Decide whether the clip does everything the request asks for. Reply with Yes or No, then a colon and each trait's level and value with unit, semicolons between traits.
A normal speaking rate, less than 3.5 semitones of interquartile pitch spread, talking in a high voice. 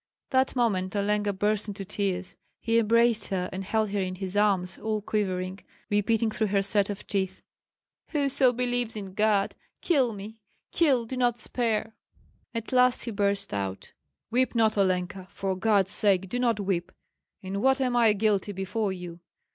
Yes: average, 165 wpm; average, 3.1 semitones; high, 210 Hz